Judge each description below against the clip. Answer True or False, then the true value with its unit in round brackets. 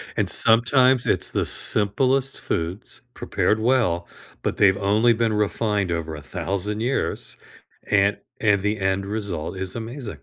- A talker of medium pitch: False (105 Hz)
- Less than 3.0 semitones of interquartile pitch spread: False (3.3 semitones)